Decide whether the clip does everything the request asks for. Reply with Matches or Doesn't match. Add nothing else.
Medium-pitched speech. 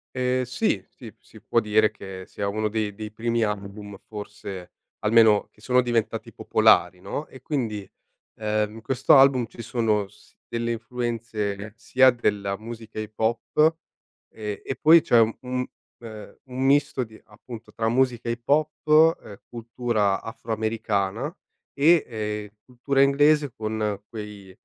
Doesn't match